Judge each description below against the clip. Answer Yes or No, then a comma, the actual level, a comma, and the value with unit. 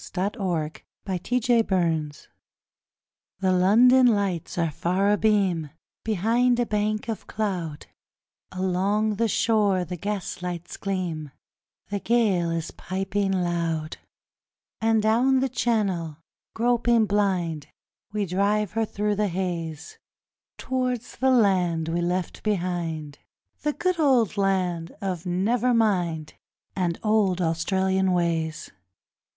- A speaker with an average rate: No, slow, 110 wpm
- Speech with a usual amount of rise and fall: Yes, average, 4.0 semitones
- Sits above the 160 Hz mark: Yes, high, 190 Hz